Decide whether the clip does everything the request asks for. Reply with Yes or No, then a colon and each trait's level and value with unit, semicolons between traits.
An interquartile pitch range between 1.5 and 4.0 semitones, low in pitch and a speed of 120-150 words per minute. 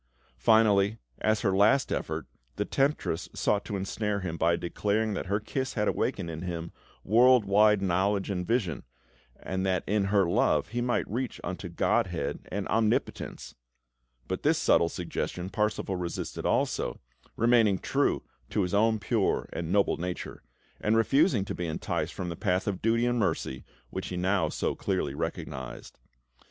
No: average, 3.4 semitones; low, 100 Hz; average, 160 wpm